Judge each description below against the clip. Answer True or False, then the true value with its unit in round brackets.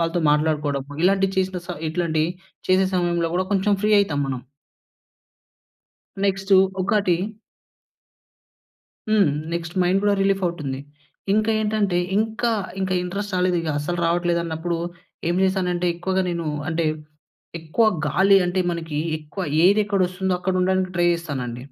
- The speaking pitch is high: False (180 Hz)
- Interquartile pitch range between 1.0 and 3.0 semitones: True (2.7 semitones)